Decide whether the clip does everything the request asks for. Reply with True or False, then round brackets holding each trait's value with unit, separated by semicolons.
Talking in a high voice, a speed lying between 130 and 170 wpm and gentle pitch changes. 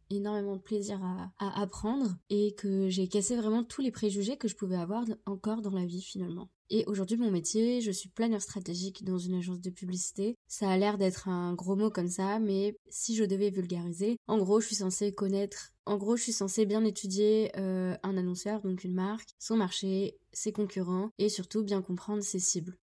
False (200 Hz; 210 wpm; 2.3 semitones)